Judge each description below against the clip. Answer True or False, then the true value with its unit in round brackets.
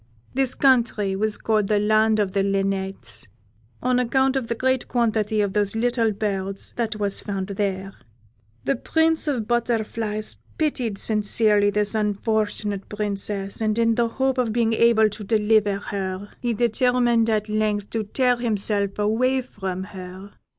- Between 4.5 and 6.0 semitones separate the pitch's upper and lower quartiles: False (2.6 semitones)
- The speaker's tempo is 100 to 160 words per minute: True (155 wpm)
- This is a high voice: True (215 Hz)